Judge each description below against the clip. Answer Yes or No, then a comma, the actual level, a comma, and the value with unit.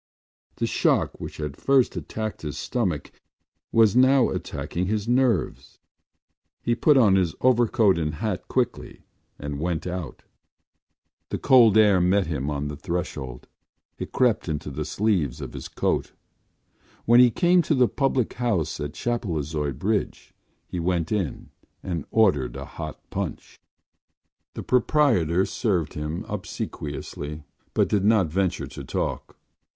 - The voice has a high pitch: No, very low, 95 Hz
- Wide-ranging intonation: Yes, wide, 7.4 semitones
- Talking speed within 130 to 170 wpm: Yes, average, 140 wpm